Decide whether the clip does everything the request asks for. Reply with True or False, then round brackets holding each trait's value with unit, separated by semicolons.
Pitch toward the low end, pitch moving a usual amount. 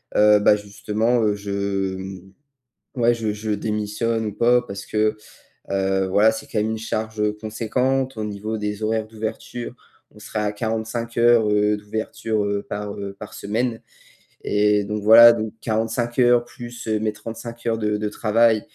False (110 Hz; 1.6 semitones)